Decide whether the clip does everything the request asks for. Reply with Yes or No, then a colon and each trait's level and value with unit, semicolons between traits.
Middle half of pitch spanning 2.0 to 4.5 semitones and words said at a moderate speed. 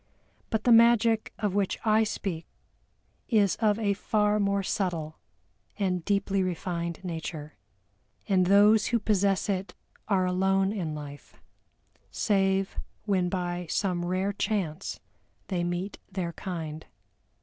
No: average, 2.8 semitones; slow, 125 wpm